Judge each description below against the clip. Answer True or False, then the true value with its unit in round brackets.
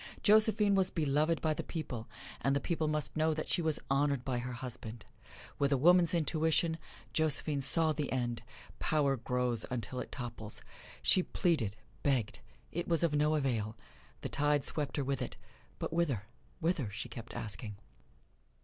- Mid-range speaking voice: True (145 Hz)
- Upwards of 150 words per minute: True (165 wpm)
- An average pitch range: True (4.4 semitones)